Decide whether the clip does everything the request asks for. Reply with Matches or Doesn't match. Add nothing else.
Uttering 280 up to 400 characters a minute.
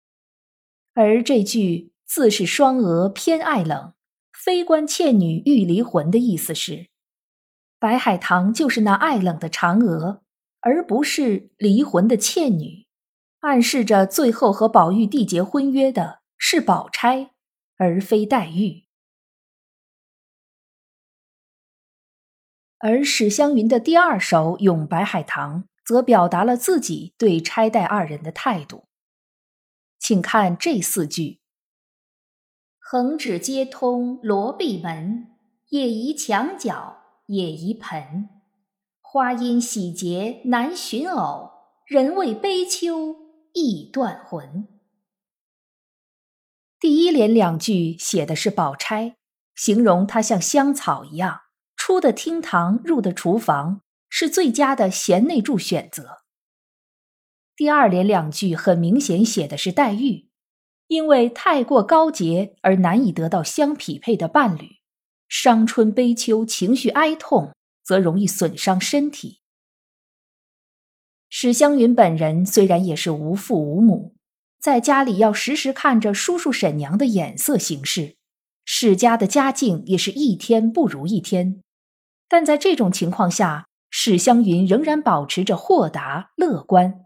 Doesn't match